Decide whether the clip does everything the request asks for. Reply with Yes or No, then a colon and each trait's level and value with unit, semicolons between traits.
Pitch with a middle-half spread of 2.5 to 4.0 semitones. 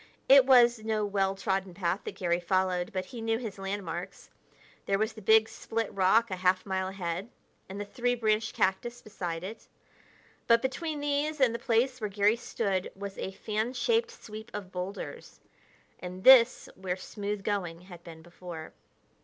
Yes: average, 3.7 semitones